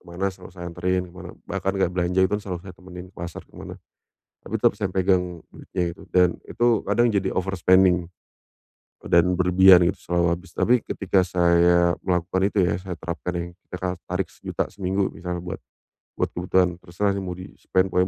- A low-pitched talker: Yes, very low, 90 Hz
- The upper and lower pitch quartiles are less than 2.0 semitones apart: Yes, narrow, 1.4 semitones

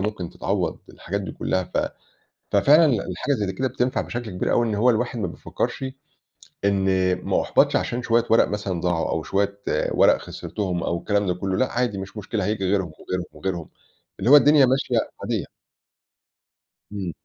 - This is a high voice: No, low, 100 Hz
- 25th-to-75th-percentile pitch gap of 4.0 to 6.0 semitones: Yes, average, 4.4 semitones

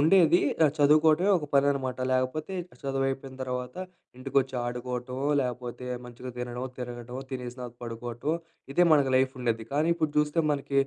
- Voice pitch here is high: No, low, 130 Hz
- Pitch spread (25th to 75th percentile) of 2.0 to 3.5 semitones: Yes, average, 2.9 semitones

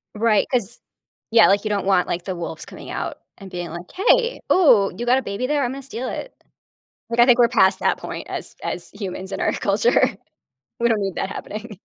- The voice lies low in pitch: No, high, 220 Hz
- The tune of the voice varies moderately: Yes, average, 4.5 semitones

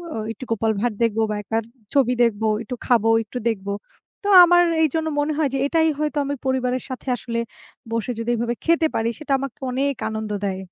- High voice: Yes, high, 245 Hz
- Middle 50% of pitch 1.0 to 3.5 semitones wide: No, average, 4.2 semitones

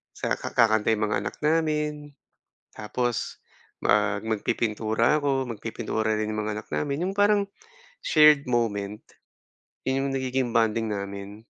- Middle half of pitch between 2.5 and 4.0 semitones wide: No, average, 5.0 semitones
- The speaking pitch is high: No, low, 115 Hz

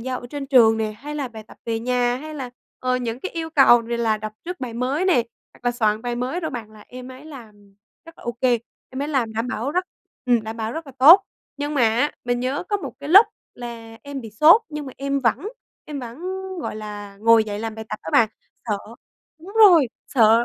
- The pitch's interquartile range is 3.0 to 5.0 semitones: Yes, average, 4.3 semitones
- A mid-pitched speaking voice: No, very high, 250 Hz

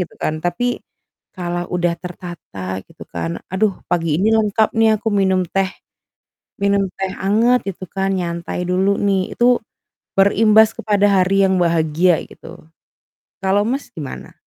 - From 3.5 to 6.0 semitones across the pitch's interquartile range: No, average, 2.8 semitones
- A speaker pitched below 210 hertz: Yes, high, 190 Hz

